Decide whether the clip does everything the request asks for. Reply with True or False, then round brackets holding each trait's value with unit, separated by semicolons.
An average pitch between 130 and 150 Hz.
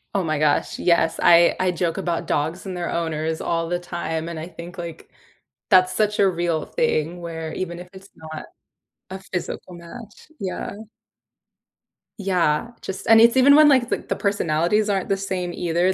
False (175 Hz)